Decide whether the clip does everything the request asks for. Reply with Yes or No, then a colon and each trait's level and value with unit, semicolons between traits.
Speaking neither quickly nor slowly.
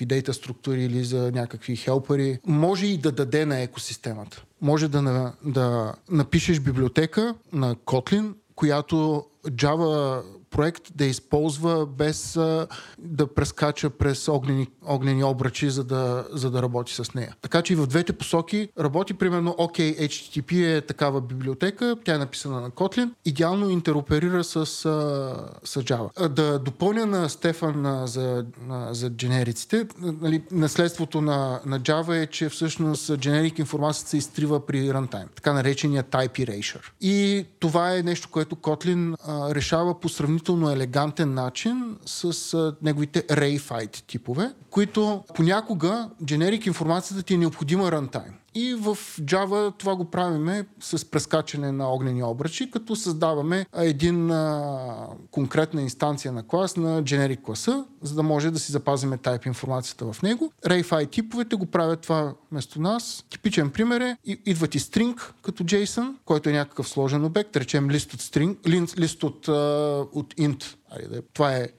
Yes: average, 150 wpm